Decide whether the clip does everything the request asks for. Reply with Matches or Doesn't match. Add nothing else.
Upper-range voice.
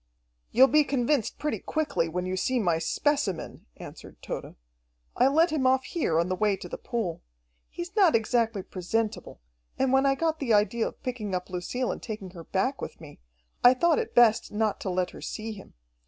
Matches